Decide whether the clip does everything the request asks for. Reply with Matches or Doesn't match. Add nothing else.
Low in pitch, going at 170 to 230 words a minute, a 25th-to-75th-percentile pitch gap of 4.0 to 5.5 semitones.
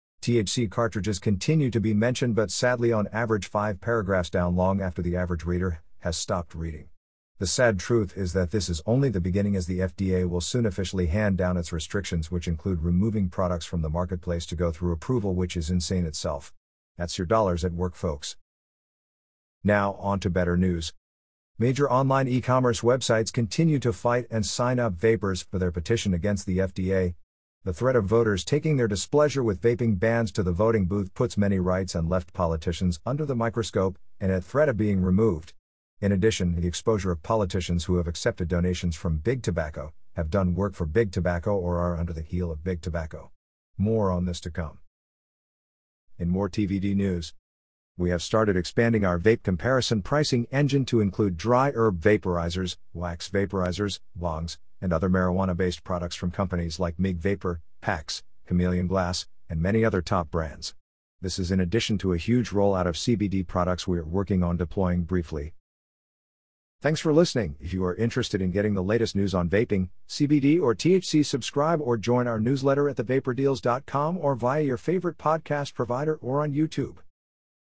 Matches